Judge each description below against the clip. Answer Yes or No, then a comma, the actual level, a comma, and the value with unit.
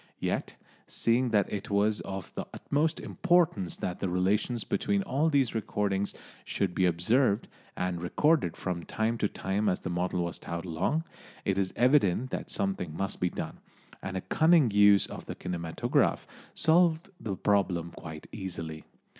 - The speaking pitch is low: Yes, low, 100 Hz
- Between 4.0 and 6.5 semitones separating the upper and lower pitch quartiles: Yes, average, 5.0 semitones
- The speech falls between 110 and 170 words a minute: Yes, average, 160 wpm